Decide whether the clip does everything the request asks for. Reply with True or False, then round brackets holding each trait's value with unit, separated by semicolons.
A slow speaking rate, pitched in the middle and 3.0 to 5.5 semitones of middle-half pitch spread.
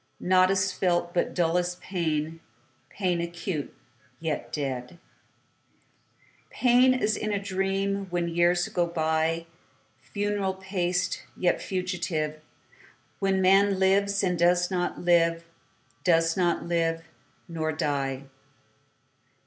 False (85 wpm; 175 Hz; 2.6 semitones)